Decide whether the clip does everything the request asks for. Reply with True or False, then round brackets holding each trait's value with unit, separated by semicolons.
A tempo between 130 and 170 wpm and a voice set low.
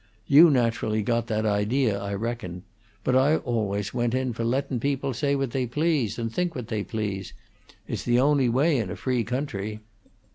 False (185 wpm; 120 Hz)